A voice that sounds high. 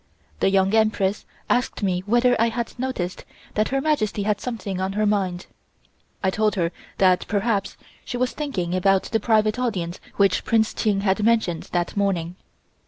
Yes: high, 205 Hz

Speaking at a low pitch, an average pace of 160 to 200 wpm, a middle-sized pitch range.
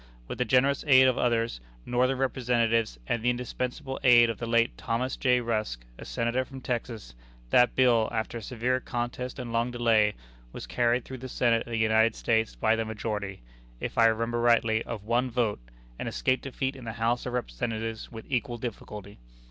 No: low, 120 Hz; average, 190 wpm; narrow, 1.8 semitones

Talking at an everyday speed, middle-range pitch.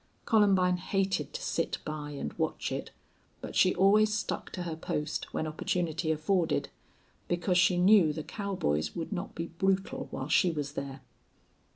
Yes: average, 160 wpm; medium, 175 Hz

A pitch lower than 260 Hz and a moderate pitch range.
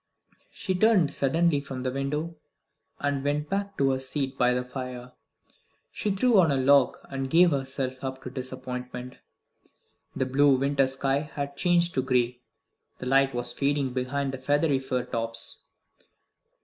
No: low, 135 Hz; narrow, 2.2 semitones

